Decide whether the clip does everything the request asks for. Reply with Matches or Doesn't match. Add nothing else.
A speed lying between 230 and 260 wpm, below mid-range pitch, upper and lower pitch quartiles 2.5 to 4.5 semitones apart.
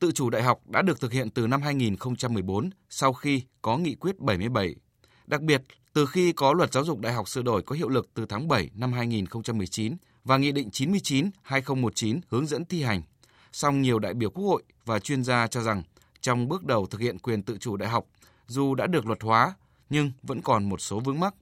Doesn't match